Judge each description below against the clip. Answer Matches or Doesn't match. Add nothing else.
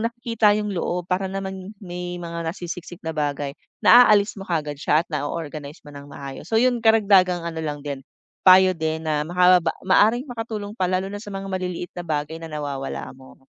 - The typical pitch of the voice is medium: Matches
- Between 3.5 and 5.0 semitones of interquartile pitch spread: Matches